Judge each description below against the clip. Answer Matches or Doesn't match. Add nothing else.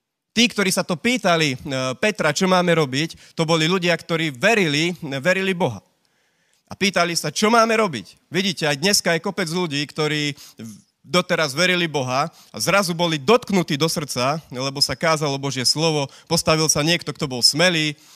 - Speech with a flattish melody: Doesn't match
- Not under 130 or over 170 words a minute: Matches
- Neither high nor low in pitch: Matches